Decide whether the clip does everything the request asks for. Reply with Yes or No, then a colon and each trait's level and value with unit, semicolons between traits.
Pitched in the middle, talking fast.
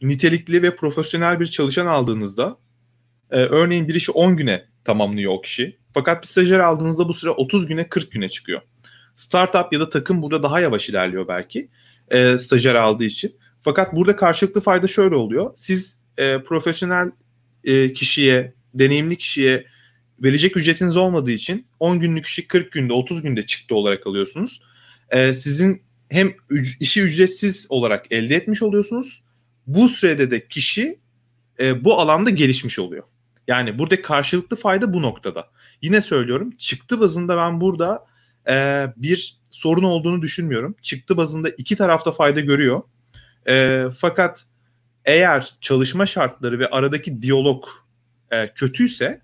Yes: medium, 145 Hz; fast, 145 wpm